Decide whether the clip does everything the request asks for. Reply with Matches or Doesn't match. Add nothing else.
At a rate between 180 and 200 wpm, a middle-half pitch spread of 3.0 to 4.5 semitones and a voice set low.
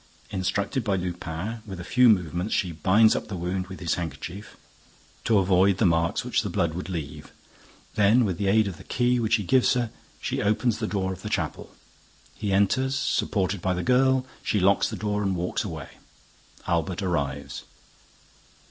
Matches